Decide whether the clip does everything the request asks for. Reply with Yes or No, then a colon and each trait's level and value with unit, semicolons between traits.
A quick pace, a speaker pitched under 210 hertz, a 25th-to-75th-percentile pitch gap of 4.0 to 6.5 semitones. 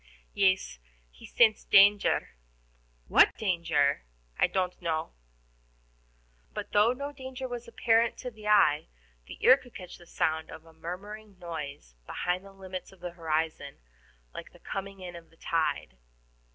No: average, 150 wpm; medium, 185 Hz; average, 4.6 semitones